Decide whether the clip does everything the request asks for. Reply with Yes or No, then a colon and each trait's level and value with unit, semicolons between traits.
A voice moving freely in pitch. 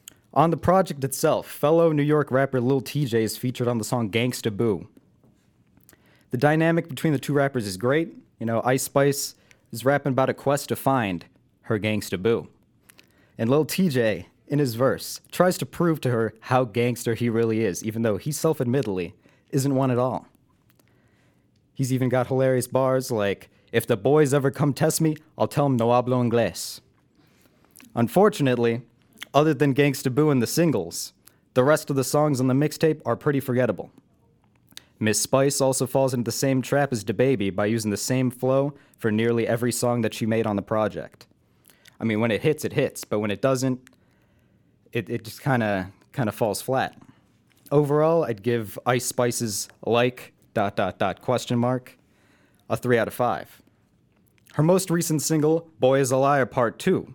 No: average, 3.6 semitones